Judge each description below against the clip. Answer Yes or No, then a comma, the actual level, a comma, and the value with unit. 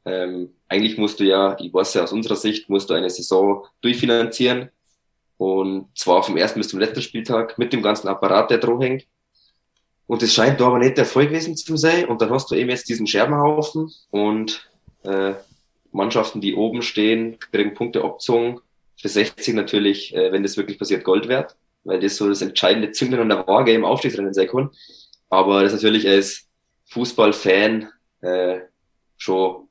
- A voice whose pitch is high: No, low, 105 Hz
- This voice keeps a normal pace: Yes, average, 180 wpm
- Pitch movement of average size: Yes, average, 3.4 semitones